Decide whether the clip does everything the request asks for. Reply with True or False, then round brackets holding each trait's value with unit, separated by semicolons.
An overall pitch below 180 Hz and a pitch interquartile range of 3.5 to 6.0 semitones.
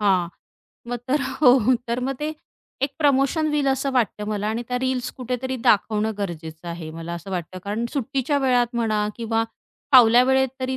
False (240 Hz; 4.2 semitones)